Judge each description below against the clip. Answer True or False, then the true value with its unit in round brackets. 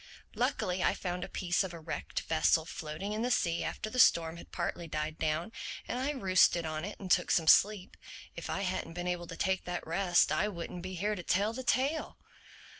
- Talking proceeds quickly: True (215 wpm)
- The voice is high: False (180 Hz)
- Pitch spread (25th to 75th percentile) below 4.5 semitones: True (3.4 semitones)